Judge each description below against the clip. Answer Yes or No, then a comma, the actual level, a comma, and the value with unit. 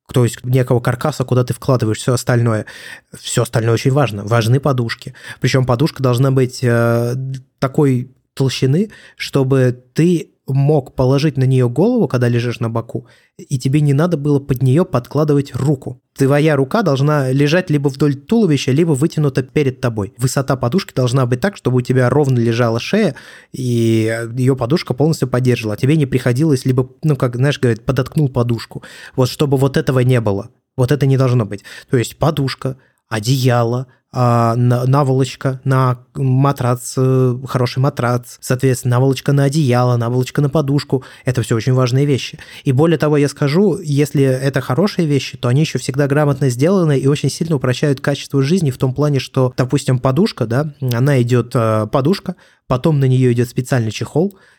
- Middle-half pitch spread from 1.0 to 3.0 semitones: Yes, average, 2.7 semitones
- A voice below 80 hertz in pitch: No, low, 135 Hz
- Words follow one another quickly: Yes, fast, 165 wpm